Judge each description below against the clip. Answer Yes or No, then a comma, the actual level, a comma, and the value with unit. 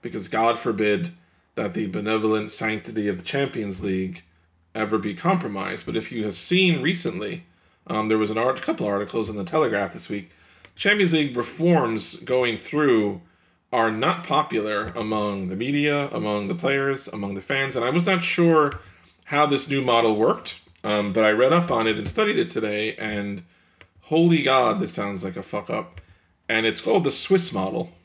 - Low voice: Yes, low, 110 Hz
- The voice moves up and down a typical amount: No, wide, 6.0 semitones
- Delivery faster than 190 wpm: No, average, 185 wpm